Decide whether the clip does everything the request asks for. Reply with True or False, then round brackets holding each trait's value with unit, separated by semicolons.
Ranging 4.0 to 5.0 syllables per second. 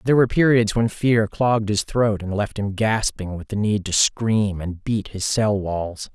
True (4.5 syllables/s)